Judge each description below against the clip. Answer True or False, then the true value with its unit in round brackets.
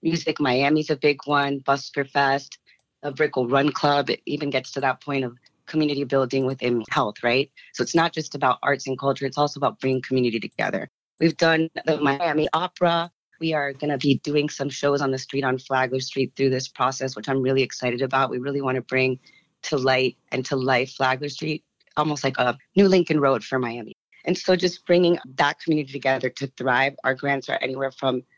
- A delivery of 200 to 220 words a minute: True (205 wpm)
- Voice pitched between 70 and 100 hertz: False (140 Hz)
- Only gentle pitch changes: True (2.2 semitones)